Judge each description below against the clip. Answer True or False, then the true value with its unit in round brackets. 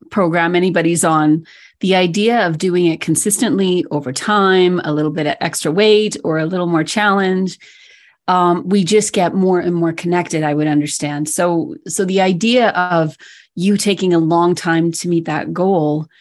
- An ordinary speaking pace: True (175 wpm)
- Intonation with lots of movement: False (3.1 semitones)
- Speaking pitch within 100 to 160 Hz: False (175 Hz)